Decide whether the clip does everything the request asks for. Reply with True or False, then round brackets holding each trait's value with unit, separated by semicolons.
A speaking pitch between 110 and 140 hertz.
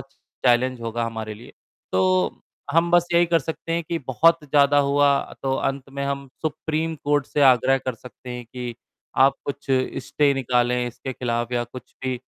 True (135 Hz)